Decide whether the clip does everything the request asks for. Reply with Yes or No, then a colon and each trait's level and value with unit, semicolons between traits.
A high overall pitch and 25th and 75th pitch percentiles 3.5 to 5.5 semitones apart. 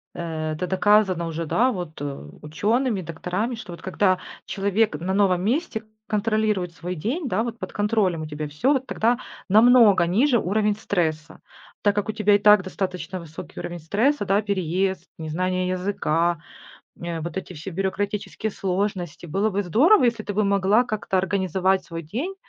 Yes: high, 195 Hz; average, 3.8 semitones